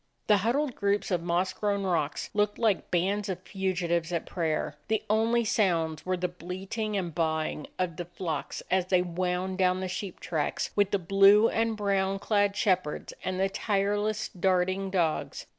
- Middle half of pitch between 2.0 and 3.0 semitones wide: Yes, narrow, 2.5 semitones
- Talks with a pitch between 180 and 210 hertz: Yes, high, 190 Hz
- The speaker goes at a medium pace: Yes, average, 175 wpm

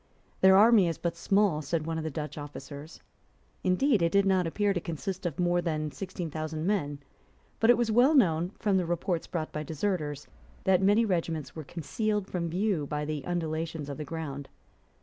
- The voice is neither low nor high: Yes, medium, 170 Hz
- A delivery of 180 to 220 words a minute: Yes, average, 190 wpm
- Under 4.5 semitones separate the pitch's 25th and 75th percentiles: Yes, average, 3.9 semitones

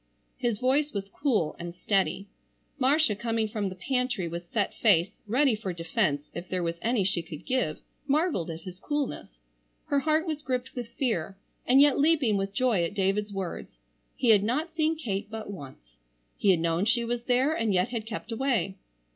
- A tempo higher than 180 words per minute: Yes, average, 190 wpm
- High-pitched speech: Yes, high, 215 Hz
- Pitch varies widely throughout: Yes, wide, 5.8 semitones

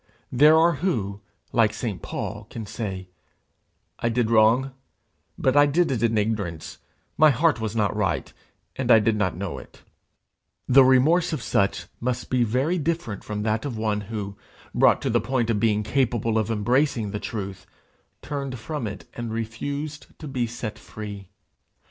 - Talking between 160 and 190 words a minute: Yes, average, 165 wpm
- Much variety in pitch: No, average, 4.1 semitones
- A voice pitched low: Yes, low, 115 Hz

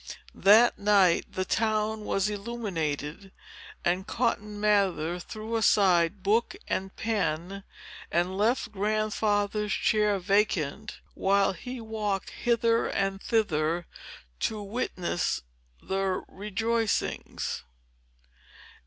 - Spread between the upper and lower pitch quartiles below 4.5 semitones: Yes, narrow, 2.5 semitones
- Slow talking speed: Yes, slow, 90 wpm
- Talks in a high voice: Yes, high, 205 Hz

